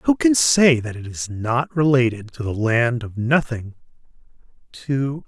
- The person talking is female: No, male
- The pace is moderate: Yes, average, 160 wpm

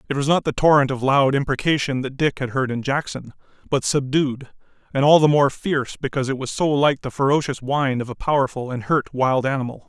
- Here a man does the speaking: Yes, male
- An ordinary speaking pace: No, fast, 220 wpm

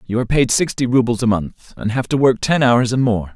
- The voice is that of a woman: No, male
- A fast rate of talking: Yes, fast, 270 wpm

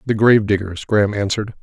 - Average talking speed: Yes, average, 185 wpm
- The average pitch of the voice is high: No, low, 105 Hz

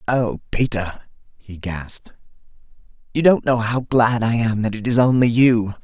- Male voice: Yes, male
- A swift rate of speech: No, average, 165 wpm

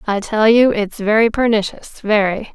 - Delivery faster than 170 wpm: No, average, 140 wpm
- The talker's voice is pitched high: Yes, high, 215 Hz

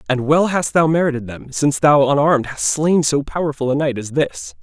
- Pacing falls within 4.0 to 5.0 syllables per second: No, 5.5 syllables/s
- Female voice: No, male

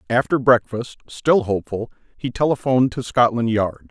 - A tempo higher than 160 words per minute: No, average, 140 wpm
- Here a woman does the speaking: No, male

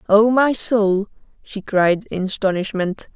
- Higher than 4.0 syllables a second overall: No, 3.9 syllables/s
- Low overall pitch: No, high, 205 Hz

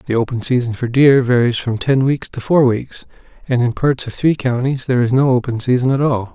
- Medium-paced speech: No, fast, 235 wpm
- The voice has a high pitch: No, low, 125 Hz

